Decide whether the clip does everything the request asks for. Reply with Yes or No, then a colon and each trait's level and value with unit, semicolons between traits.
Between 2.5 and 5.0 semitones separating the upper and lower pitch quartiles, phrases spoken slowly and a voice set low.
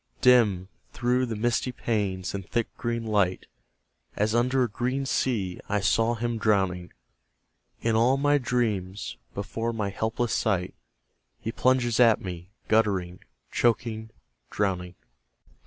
Yes: average, 3.6 semitones; slow, 125 wpm; low, 110 Hz